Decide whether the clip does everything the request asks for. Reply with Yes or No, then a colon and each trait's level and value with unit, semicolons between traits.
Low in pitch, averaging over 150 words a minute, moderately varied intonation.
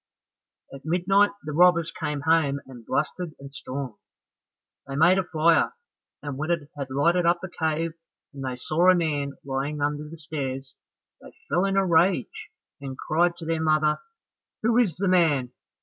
No: medium, 155 Hz; average, 170 wpm; average, 3.5 semitones